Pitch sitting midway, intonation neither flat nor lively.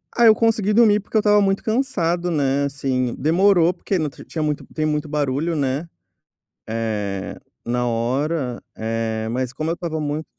No: medium, 150 Hz; wide, 5.7 semitones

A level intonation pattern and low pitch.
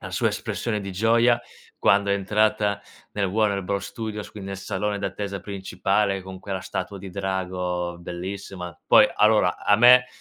Yes: narrow, 1.8 semitones; low, 100 Hz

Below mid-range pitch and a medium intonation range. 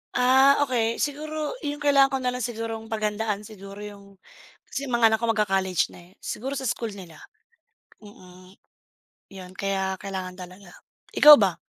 No: high, 215 Hz; average, 4.7 semitones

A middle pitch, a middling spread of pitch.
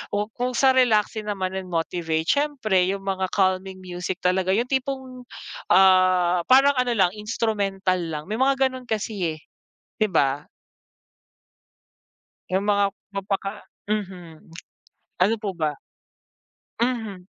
No: high, 195 Hz; average, 3.7 semitones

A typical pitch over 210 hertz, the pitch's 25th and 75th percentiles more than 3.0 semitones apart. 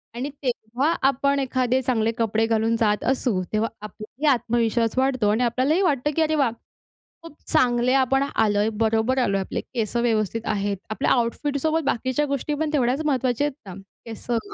Yes: high, 245 Hz; average, 3.6 semitones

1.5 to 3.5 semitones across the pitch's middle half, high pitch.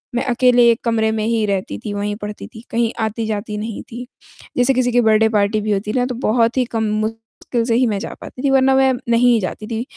Yes: narrow, 2.5 semitones; high, 230 Hz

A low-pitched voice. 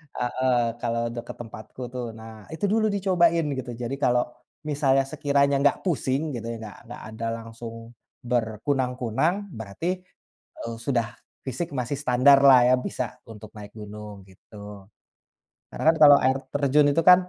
Yes: low, 125 Hz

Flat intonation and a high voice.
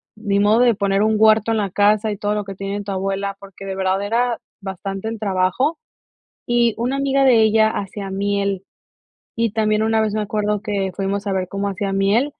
Yes: narrow, 2.0 semitones; high, 205 Hz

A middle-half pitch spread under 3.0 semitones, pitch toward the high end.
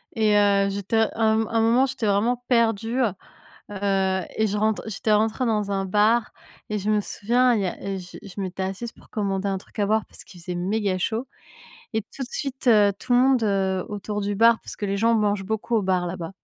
Yes: narrow, 2.4 semitones; high, 210 Hz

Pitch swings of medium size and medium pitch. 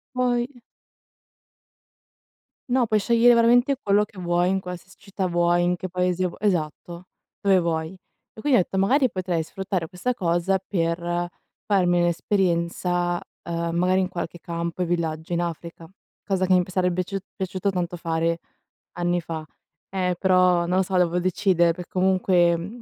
No: narrow, 2.0 semitones; medium, 180 Hz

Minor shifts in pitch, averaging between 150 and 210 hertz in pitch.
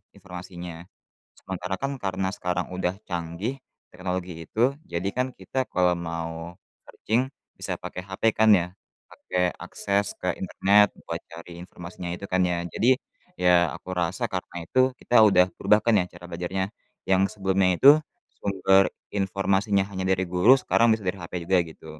No: narrow, 1.9 semitones; very low, 95 Hz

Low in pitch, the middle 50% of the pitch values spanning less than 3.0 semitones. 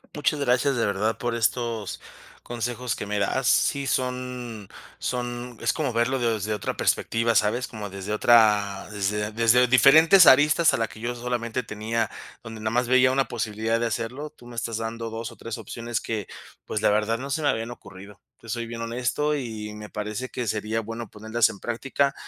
Yes: low, 115 Hz; narrow, 2.5 semitones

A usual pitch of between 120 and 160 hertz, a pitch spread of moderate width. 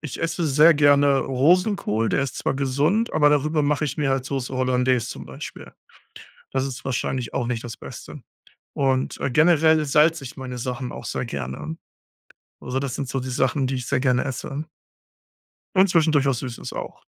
Yes: low, 135 Hz; average, 3.0 semitones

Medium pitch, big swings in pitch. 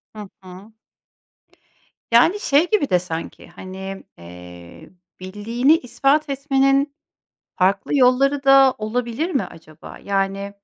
No: high, 235 Hz; wide, 6.6 semitones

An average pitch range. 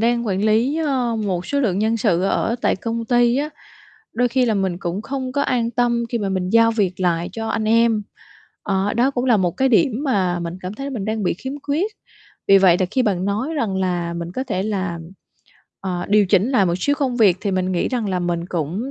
Yes: average, 4.7 semitones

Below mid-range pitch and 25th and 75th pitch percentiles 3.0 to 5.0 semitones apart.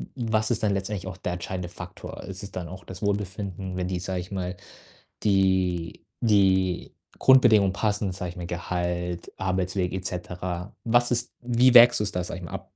No: very low, 95 Hz; narrow, 2.5 semitones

